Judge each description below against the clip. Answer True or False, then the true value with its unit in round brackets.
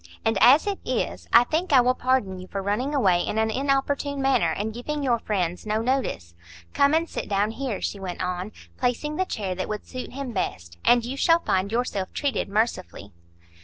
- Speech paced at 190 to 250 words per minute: True (200 wpm)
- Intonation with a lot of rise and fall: True (5.8 semitones)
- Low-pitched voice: False (235 Hz)